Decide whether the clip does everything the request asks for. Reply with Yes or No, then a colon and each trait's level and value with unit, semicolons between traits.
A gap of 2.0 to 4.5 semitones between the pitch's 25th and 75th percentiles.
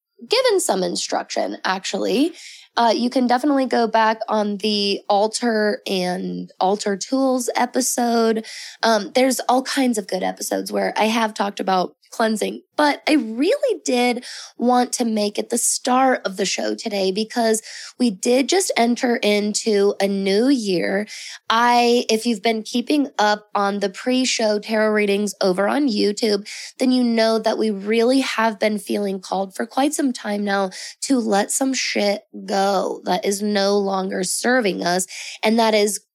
Yes: average, 3.6 semitones